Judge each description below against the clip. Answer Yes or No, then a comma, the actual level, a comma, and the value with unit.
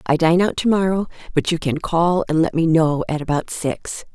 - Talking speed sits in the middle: No, fast, 230 wpm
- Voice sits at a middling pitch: Yes, medium, 165 Hz